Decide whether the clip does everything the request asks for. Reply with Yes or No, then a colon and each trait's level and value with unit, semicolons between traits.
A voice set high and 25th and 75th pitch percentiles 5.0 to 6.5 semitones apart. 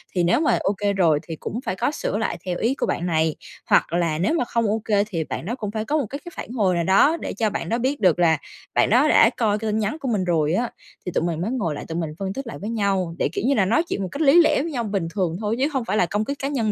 Yes: high, 210 Hz; wide, 5.5 semitones